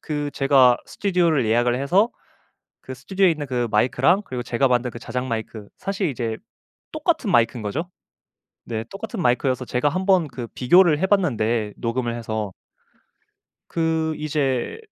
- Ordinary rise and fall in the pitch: No, wide, 6.5 semitones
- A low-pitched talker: Yes, low, 130 Hz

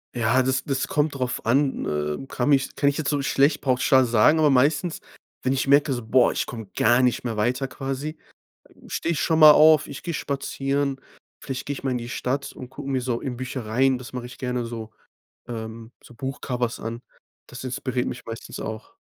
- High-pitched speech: No, low, 130 Hz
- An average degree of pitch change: No, narrow, 2.3 semitones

